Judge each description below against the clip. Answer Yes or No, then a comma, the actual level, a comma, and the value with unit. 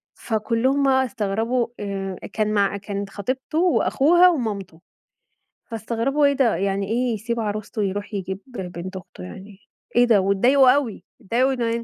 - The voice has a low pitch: No, high, 225 Hz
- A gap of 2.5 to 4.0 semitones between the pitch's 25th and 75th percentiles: No, average, 4.4 semitones